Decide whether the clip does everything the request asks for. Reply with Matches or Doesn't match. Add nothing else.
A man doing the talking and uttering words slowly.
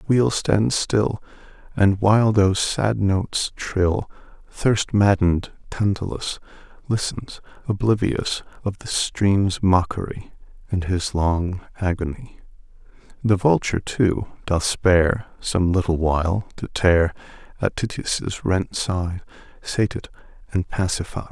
Matches